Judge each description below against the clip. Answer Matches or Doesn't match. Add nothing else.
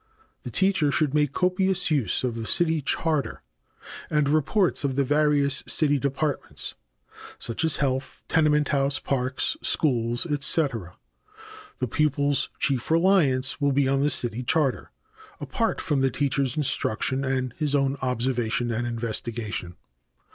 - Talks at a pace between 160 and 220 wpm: Doesn't match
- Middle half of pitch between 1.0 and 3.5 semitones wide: Matches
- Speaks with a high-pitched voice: Doesn't match